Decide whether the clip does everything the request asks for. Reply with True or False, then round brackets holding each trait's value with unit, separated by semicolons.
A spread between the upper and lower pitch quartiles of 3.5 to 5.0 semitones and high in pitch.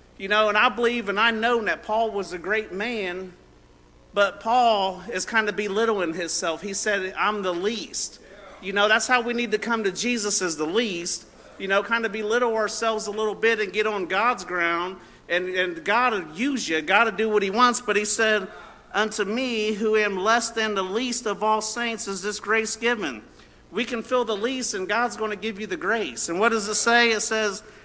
False (2.7 semitones; 215 Hz)